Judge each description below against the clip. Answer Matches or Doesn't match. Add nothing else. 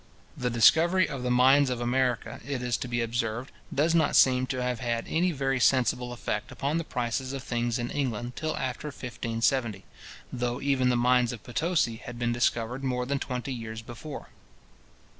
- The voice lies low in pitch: Matches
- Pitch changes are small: Matches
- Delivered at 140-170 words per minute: Doesn't match